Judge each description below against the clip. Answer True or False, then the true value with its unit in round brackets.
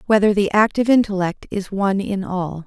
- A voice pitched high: True (200 Hz)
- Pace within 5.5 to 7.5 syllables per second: True (5.7 syllables/s)